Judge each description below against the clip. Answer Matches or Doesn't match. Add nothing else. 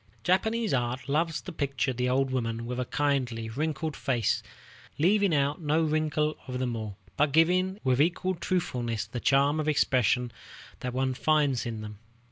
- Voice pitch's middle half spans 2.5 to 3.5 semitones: Doesn't match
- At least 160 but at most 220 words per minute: Matches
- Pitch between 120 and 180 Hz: Matches